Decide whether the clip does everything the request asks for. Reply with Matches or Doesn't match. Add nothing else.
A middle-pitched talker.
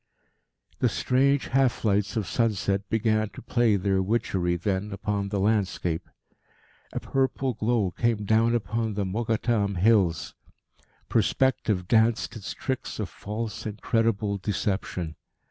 Doesn't match